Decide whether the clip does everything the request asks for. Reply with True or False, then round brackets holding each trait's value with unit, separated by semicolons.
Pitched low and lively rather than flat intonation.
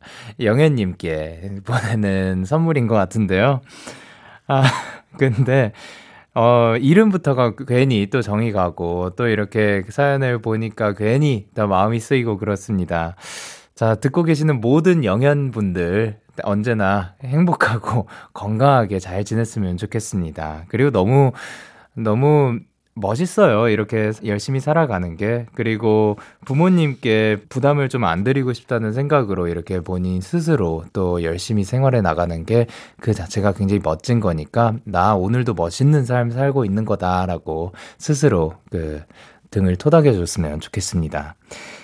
True (110 Hz; 5.8 semitones)